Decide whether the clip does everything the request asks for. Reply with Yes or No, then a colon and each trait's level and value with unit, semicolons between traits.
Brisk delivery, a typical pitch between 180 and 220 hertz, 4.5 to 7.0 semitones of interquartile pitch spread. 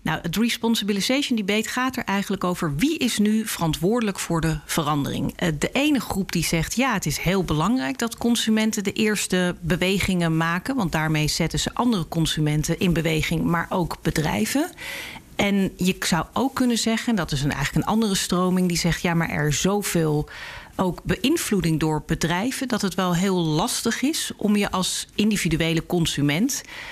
No: average, 170 wpm; medium, 185 Hz; wide, 5.4 semitones